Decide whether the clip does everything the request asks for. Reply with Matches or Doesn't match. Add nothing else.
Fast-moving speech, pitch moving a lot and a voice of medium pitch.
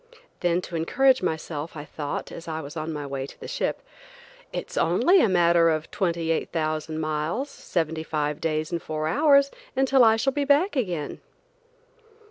Doesn't match